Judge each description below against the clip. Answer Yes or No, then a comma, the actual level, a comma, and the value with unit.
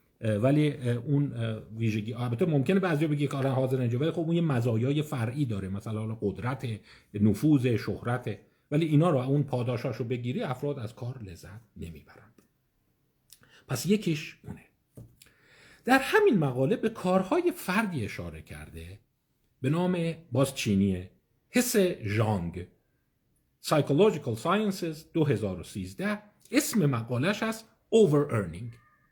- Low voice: Yes, low, 130 Hz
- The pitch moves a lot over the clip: Yes, wide, 6.7 semitones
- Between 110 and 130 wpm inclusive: Yes, average, 120 wpm